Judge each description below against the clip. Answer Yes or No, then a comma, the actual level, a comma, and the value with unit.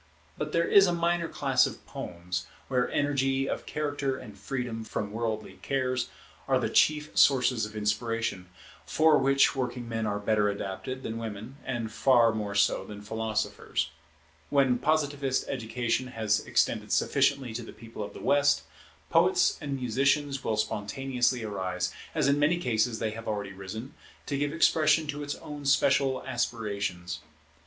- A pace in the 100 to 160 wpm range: Yes, average, 155 wpm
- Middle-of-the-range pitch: No, low, 125 Hz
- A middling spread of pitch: Yes, average, 4.4 semitones